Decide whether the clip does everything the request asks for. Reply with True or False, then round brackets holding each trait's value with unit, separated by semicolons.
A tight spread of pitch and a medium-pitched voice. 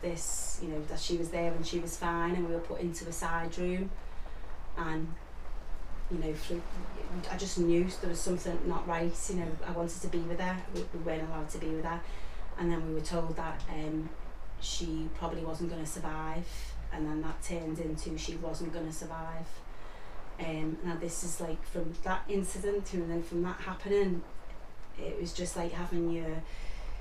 True (1.5 semitones; 165 Hz)